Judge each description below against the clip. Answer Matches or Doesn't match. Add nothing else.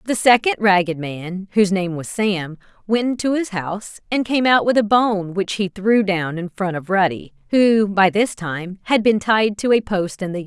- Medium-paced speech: Doesn't match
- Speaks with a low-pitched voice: Doesn't match